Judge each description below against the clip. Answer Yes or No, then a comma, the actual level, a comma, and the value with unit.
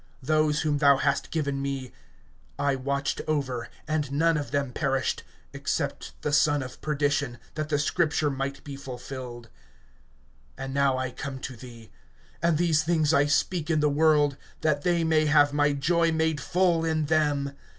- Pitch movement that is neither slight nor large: No, narrow, 2.1 semitones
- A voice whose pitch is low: No, medium, 145 Hz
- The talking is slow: No, average, 165 wpm